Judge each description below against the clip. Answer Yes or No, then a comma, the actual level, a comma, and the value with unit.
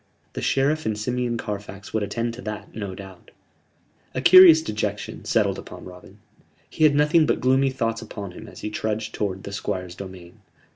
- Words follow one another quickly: No, average, 180 wpm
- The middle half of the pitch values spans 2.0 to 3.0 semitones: No, average, 4.6 semitones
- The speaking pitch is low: Yes, low, 110 Hz